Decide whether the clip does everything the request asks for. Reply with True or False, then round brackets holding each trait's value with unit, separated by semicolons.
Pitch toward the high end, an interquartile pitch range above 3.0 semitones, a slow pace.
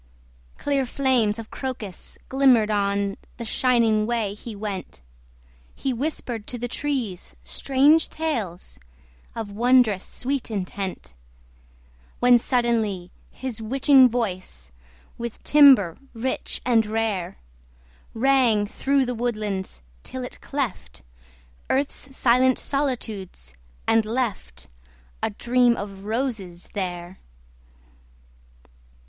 True (230 Hz; 4.4 semitones; 100 wpm)